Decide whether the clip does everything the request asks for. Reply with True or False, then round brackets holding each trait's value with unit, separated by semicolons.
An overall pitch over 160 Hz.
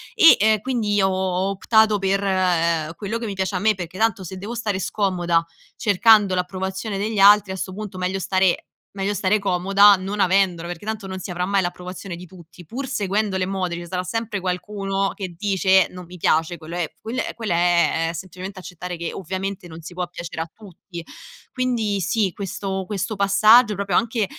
True (190 Hz)